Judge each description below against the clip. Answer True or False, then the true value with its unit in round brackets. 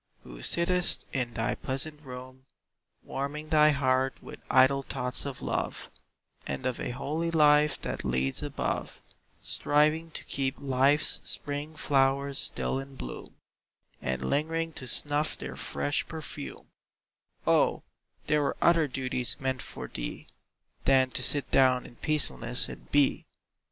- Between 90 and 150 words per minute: True (135 wpm)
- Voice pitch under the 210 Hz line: True (135 Hz)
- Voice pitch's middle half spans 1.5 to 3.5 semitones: True (2.8 semitones)